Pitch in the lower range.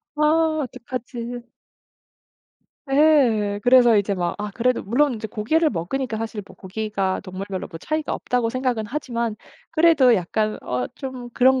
No: high, 235 Hz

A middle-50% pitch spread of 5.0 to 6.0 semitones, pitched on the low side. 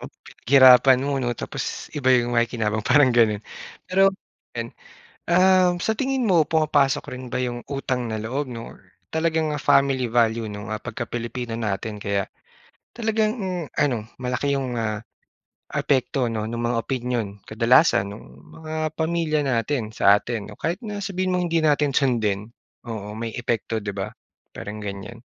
Yes: wide, 5.4 semitones; low, 125 Hz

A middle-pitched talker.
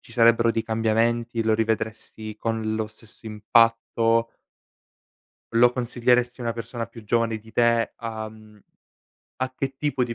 No: low, 115 Hz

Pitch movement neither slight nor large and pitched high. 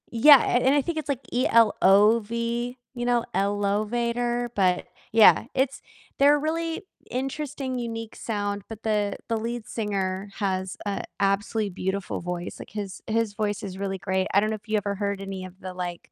Yes: average, 3.4 semitones; high, 215 Hz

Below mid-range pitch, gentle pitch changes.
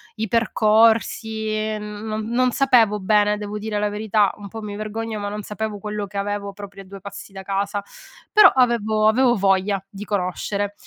No: high, 210 Hz; narrow, 1.4 semitones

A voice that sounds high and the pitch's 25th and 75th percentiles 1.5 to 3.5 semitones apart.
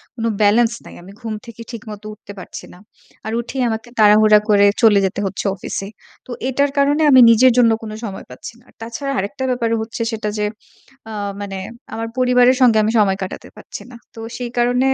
Yes: high, 225 Hz; average, 2.9 semitones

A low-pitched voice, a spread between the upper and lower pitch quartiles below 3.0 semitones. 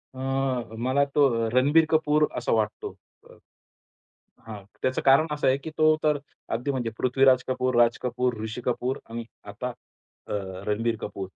No: low, 130 Hz; average, 3.3 semitones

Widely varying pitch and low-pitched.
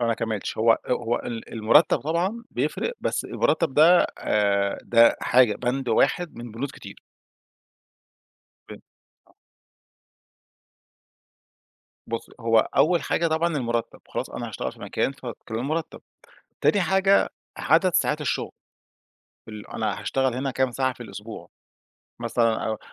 Yes: wide, 5.7 semitones; low, 125 Hz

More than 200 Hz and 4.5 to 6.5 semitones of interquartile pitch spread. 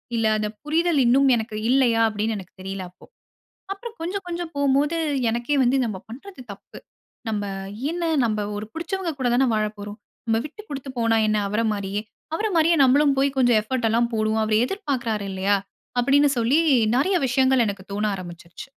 Yes: high, 240 Hz; average, 5.1 semitones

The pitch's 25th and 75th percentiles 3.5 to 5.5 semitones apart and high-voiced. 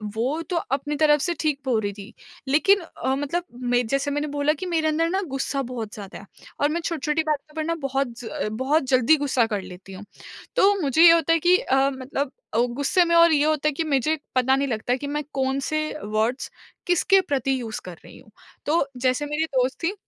Yes: average, 3.8 semitones; very high, 280 Hz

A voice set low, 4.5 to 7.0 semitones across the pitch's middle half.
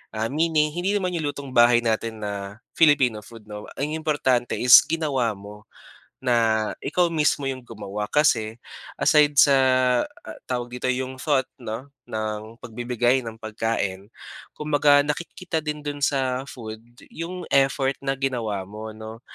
Yes: low, 125 Hz; average, 4.8 semitones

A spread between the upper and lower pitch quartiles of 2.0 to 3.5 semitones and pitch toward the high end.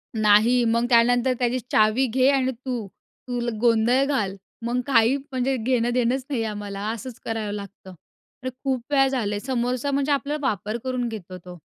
Yes: average, 2.9 semitones; high, 240 Hz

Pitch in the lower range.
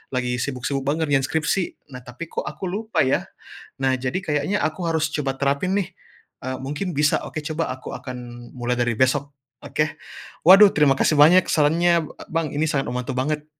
No: medium, 145 Hz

